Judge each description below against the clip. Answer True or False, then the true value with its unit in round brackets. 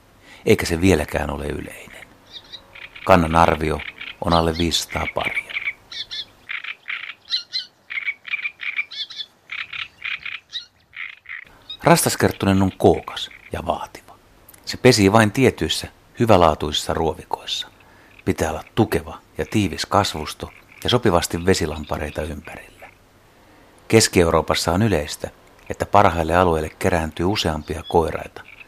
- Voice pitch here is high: False (90 Hz)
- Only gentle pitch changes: False (4.1 semitones)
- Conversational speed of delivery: False (85 wpm)